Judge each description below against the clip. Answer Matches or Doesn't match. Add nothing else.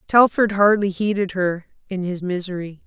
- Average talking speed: Matches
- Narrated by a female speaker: Matches